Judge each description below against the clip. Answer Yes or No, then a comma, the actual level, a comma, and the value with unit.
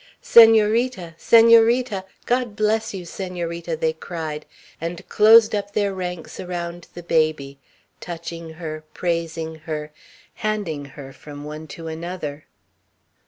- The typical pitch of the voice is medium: Yes, medium, 170 Hz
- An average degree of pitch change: Yes, average, 4.6 semitones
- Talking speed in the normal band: No, slow, 115 wpm